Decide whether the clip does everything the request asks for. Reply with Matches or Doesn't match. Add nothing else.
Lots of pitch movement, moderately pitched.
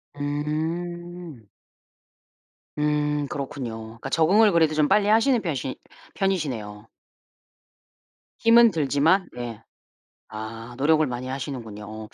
Matches